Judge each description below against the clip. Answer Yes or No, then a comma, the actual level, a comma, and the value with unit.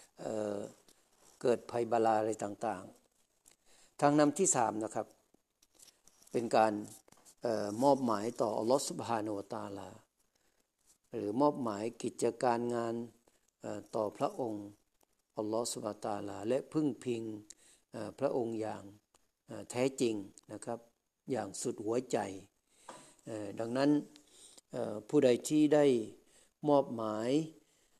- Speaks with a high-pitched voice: No, low, 115 Hz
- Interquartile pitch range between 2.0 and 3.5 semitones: Yes, average, 2.8 semitones